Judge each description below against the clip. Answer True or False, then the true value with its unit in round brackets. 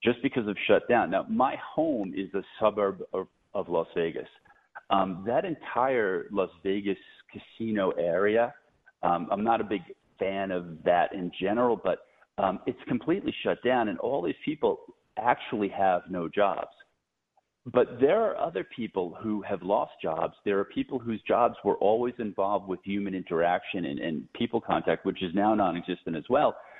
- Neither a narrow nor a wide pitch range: False (2.3 semitones)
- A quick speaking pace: False (170 wpm)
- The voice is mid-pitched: False (100 Hz)